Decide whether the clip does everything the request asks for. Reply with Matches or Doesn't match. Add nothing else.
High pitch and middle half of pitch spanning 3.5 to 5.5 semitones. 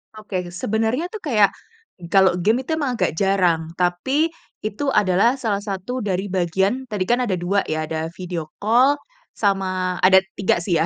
Matches